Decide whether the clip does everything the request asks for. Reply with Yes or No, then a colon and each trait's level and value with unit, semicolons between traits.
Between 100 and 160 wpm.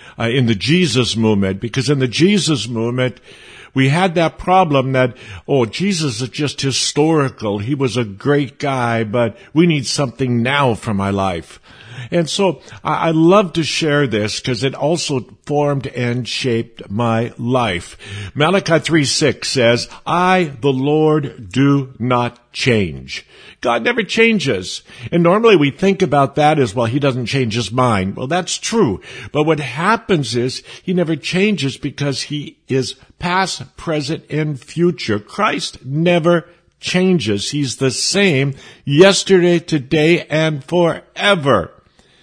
Yes: average, 140 wpm